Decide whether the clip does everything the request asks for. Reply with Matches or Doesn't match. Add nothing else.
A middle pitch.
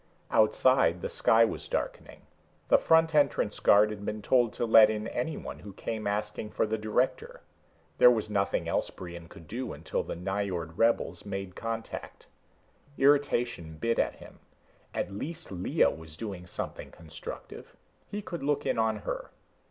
Doesn't match